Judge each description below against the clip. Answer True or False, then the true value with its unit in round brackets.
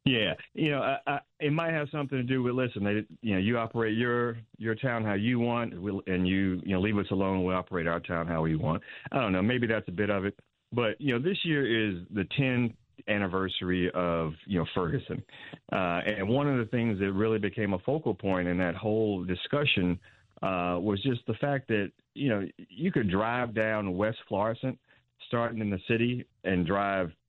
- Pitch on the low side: True (105 Hz)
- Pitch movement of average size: True (4.2 semitones)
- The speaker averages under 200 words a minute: False (205 wpm)